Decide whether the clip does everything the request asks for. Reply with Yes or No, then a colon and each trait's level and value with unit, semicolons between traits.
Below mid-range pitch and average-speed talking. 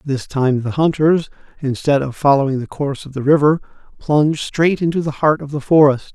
No: medium, 145 Hz; average, 195 wpm